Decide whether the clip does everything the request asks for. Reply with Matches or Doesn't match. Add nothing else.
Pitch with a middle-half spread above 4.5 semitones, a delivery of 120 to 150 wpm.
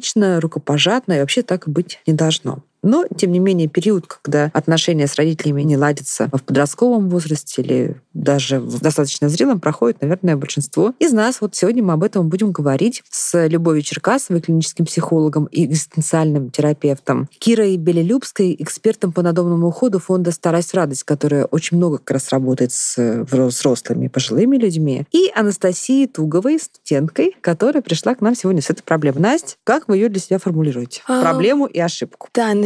Doesn't match